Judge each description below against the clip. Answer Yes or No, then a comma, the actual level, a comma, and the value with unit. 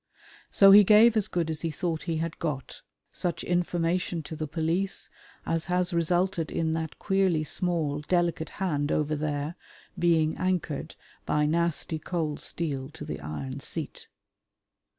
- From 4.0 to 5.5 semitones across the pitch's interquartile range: No, narrow, 2.5 semitones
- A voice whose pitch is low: No, medium, 165 Hz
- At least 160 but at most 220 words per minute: No, average, 150 wpm